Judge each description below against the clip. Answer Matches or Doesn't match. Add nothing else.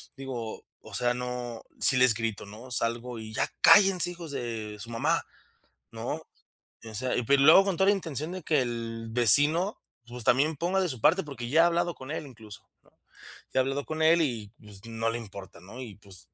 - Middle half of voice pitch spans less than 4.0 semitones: Doesn't match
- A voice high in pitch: Doesn't match